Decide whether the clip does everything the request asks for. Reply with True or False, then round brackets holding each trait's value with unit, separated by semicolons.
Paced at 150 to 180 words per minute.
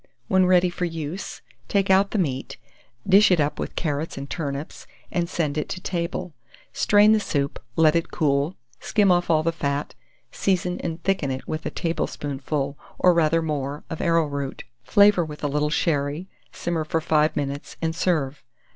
True (175 wpm)